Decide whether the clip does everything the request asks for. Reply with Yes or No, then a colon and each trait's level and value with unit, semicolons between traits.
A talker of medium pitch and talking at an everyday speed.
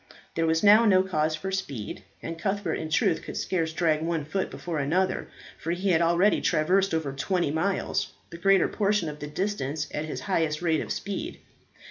Yes: medium, 170 Hz; average, 190 wpm